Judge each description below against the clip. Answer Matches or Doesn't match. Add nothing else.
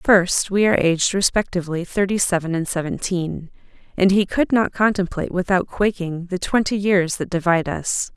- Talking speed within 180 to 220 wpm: Doesn't match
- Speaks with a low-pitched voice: Doesn't match